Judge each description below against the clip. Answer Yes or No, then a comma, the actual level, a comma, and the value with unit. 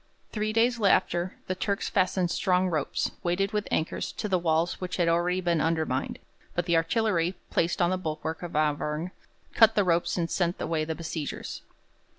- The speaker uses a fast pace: No, average, 175 wpm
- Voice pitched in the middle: Yes, medium, 175 Hz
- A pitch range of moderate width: No, narrow, 2.3 semitones